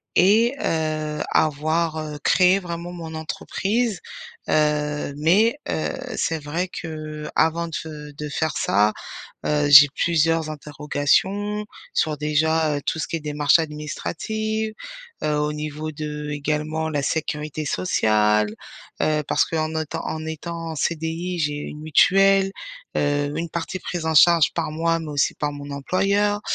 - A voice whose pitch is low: No, medium, 155 Hz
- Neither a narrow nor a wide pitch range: No, narrow, 2.2 semitones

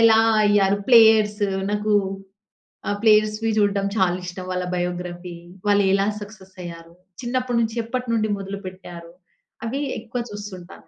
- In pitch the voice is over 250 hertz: No, high, 205 Hz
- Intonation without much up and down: No, average, 3.2 semitones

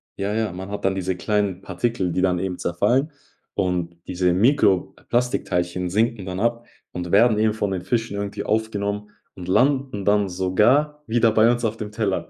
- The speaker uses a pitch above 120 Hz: No, low, 100 Hz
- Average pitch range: Yes, average, 3.6 semitones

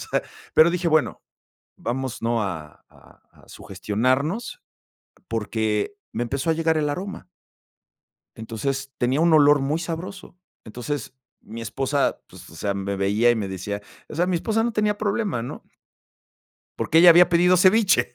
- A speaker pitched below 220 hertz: Yes, medium, 140 Hz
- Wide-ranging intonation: Yes, wide, 7.4 semitones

